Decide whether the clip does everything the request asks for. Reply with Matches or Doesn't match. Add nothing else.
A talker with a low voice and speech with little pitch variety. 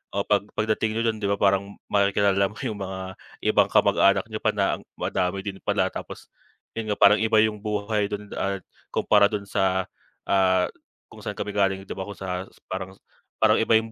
Matches